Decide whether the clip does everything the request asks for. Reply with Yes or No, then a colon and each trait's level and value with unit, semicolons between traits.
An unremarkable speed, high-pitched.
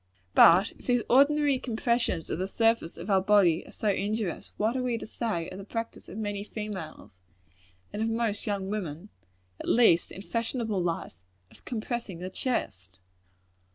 Yes: average, 170 wpm; high, 210 Hz